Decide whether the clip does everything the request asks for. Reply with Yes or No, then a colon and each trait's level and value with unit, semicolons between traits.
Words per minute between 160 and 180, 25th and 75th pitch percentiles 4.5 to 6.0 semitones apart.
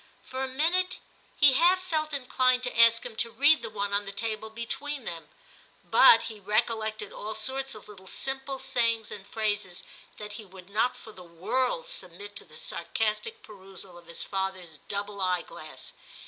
Yes: average, 175 wpm; average, 4.9 semitones